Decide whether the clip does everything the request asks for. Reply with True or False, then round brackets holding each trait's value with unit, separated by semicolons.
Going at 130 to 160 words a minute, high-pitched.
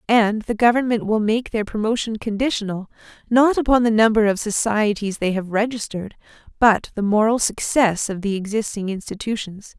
True (155 wpm; 215 Hz)